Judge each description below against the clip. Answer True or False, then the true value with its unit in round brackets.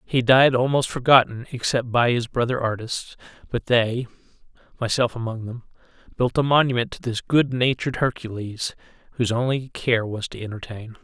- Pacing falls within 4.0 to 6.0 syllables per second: True (5.0 syllables/s)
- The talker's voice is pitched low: True (120 Hz)